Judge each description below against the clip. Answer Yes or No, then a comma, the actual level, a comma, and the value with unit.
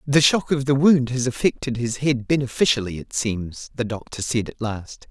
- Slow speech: No, average, 200 wpm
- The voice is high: No, low, 125 Hz